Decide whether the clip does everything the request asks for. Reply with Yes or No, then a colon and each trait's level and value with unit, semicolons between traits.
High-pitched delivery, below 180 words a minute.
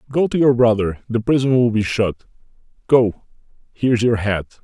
No: low, 115 Hz; average, 170 wpm